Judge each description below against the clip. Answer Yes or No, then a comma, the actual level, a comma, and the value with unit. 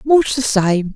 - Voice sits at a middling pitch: No, high, 230 Hz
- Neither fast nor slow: Yes, average, 190 wpm